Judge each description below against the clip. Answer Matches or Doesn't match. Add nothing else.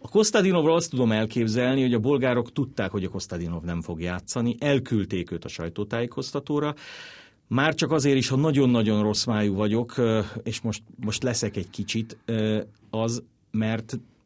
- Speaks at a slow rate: Doesn't match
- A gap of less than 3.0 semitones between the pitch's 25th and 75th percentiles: Doesn't match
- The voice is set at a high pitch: Doesn't match